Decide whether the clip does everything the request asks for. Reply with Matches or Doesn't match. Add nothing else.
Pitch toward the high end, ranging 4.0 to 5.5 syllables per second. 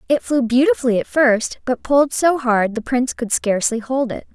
Matches